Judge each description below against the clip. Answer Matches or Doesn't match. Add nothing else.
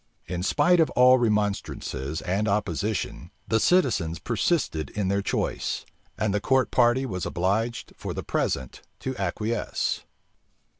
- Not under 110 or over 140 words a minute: Matches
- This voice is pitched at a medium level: Doesn't match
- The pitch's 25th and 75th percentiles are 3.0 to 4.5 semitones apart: Doesn't match